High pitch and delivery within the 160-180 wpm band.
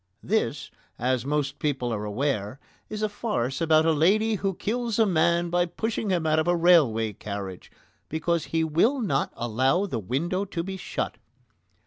No: medium, 160 Hz; average, 170 wpm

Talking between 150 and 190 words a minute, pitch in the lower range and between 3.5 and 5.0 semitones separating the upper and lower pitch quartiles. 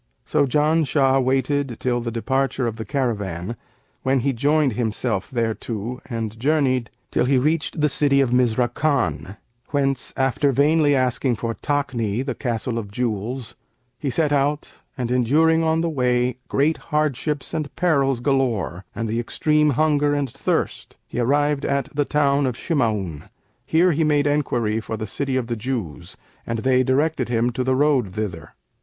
Yes: average, 160 wpm; low, 130 Hz; average, 3.8 semitones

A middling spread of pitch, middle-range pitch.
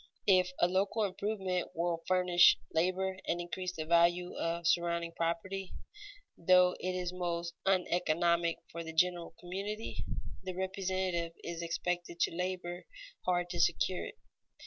No: narrow, 1.5 semitones; medium, 180 Hz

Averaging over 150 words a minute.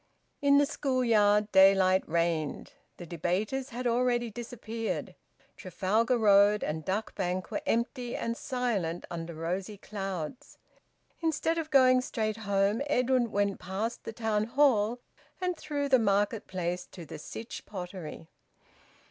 No: slow, 135 wpm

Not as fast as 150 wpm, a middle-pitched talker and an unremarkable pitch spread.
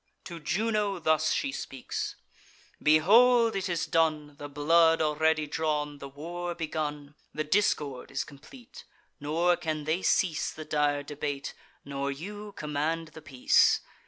Yes: slow, 135 wpm; medium, 155 Hz; average, 3.0 semitones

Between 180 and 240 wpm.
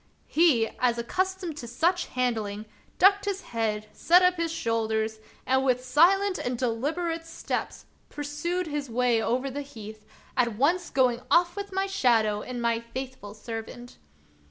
No: average, 170 wpm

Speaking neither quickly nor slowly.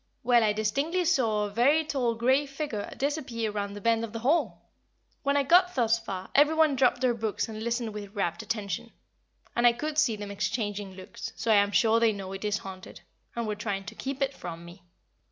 No: fast, 215 wpm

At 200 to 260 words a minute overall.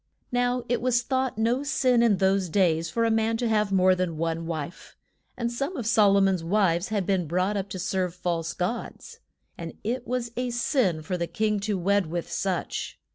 Yes: fast, 205 wpm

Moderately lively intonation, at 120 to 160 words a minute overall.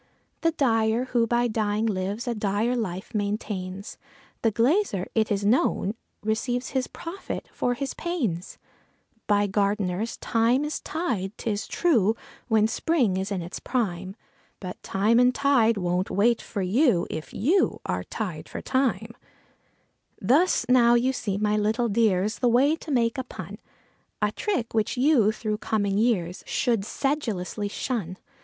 Yes: average, 3.6 semitones; average, 150 wpm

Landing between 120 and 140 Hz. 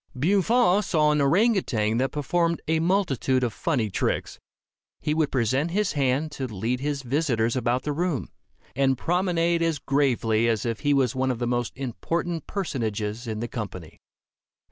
Yes: low, 135 Hz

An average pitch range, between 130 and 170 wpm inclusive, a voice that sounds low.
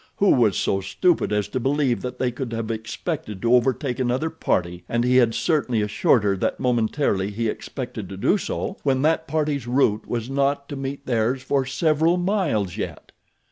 No: average, 4.3 semitones; average, 185 wpm; low, 125 Hz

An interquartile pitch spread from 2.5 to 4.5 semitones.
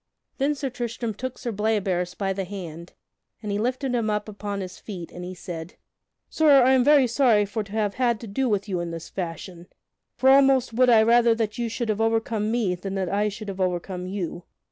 Yes: average, 4.2 semitones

